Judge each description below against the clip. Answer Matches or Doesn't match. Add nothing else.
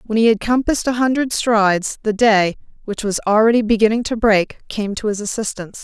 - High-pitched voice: Matches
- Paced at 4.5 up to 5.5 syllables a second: Doesn't match